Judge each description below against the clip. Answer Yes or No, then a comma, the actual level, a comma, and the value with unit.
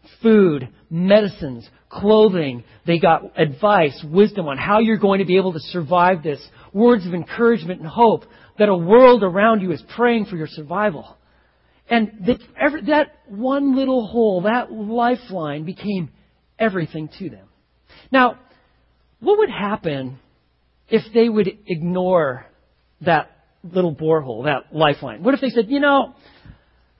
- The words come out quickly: No, average, 140 wpm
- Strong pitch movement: Yes, wide, 6.5 semitones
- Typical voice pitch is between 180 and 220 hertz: Yes, high, 190 Hz